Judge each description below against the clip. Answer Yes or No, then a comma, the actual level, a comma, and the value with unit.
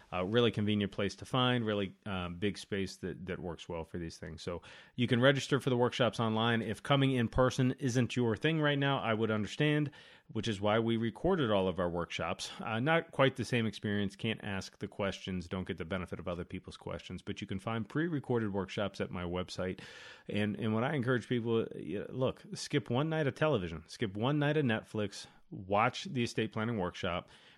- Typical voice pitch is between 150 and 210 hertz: No, low, 110 Hz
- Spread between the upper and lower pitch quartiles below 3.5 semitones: No, average, 4.8 semitones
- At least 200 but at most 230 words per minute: Yes, fast, 205 wpm